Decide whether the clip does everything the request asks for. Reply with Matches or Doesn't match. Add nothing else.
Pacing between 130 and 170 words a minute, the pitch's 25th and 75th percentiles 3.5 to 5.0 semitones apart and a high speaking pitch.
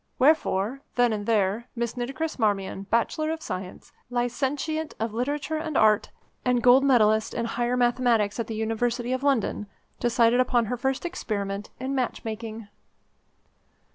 Doesn't match